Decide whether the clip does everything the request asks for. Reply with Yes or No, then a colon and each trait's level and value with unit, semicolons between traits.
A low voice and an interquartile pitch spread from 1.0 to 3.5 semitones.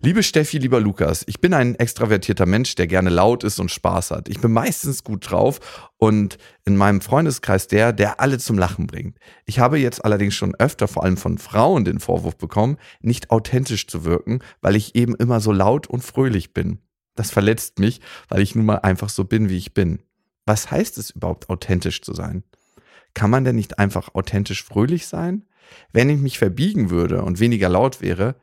No: low, 105 Hz; average, 4.2 semitones